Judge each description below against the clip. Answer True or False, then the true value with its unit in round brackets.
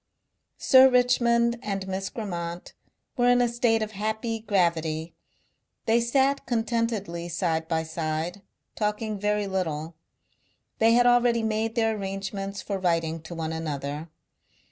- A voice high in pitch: True (205 Hz)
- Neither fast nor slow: False (130 wpm)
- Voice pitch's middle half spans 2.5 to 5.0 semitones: False (5.4 semitones)